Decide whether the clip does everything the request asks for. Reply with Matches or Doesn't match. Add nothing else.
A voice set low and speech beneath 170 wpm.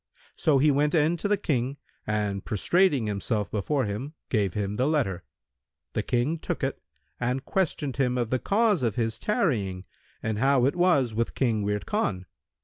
Doesn't match